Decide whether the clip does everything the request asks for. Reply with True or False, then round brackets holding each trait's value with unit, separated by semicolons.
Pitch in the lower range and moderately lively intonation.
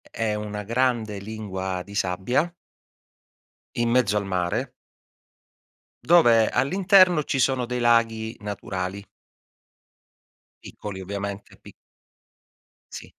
True (110 Hz; 3.8 semitones)